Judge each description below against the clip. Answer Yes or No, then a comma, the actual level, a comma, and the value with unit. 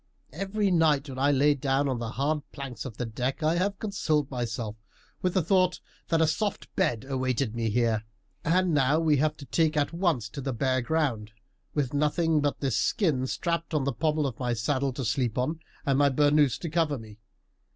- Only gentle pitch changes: No, average, 4.0 semitones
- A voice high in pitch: No, medium, 145 Hz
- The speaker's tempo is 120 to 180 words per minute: No, fast, 205 wpm